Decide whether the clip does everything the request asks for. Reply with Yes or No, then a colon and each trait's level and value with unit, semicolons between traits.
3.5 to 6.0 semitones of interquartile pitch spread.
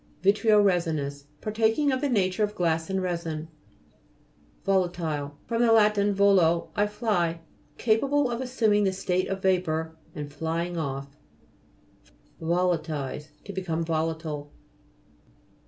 Yes: average, 4.4 semitones